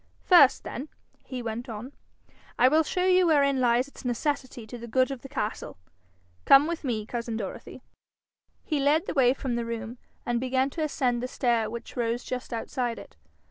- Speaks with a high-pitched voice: Yes, very high, 255 Hz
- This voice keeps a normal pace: Yes, average, 185 wpm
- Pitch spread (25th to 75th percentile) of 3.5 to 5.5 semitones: No, average, 3.0 semitones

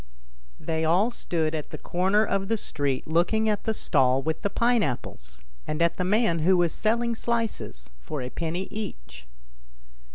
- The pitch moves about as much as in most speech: No, wide, 6.1 semitones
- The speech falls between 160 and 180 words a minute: Yes, average, 170 wpm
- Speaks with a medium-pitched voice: Yes, medium, 175 Hz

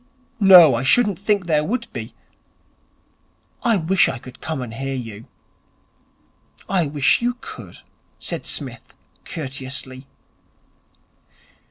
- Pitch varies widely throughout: Yes, wide, 6.8 semitones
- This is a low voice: No, medium, 150 Hz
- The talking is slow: Yes, slow, 115 wpm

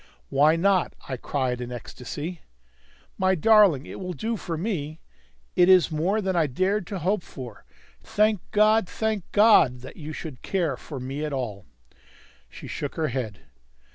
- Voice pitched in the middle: Yes, medium, 165 Hz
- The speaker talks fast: No, average, 170 wpm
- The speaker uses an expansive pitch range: Yes, wide, 6.6 semitones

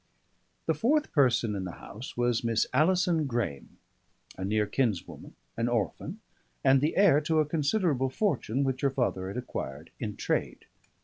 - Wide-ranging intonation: Yes, wide, 5.9 semitones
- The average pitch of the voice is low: Yes, low, 130 Hz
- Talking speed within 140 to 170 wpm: Yes, average, 160 wpm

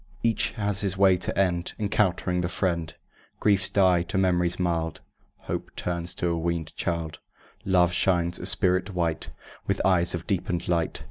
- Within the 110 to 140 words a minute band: No, average, 155 wpm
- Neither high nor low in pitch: No, very low, 90 Hz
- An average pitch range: No, narrow, 1.8 semitones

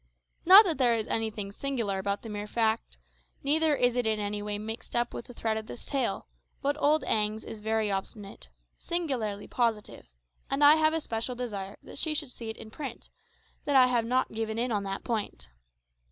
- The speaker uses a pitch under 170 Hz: No, high, 225 Hz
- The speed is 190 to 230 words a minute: Yes, average, 200 wpm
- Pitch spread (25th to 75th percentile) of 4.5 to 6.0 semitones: No, average, 4.1 semitones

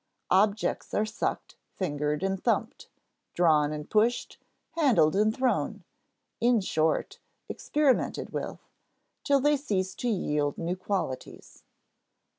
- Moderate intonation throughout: No, wide, 7.1 semitones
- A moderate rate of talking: No, slow, 110 wpm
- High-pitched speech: Yes, high, 200 Hz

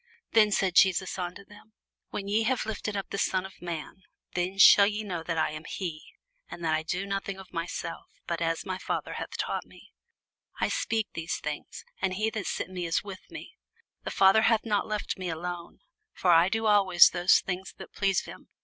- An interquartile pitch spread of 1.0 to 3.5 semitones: Yes, average, 3.0 semitones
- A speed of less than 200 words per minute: No, fast, 205 wpm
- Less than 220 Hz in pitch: Yes, high, 190 Hz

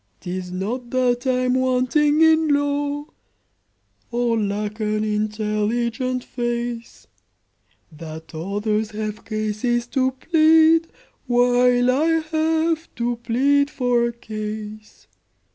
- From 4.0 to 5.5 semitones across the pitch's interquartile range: Yes, average, 4.5 semitones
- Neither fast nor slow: No, slow, 100 wpm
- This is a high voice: Yes, high, 240 Hz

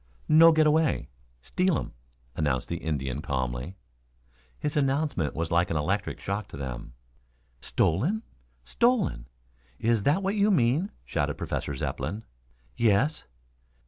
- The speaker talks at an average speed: No, slow, 125 wpm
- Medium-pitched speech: No, low, 105 Hz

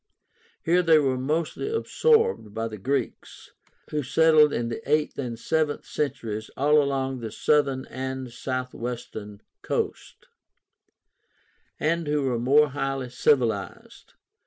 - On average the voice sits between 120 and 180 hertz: Yes, low, 135 Hz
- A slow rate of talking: Yes, slow, 120 wpm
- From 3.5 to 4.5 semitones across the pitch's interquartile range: Yes, average, 3.8 semitones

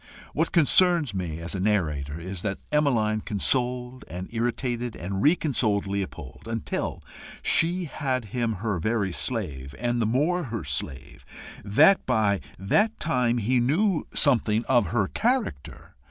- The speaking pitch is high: No, low, 115 Hz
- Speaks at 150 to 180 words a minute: No, average, 140 wpm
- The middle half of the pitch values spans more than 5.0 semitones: Yes, wide, 5.4 semitones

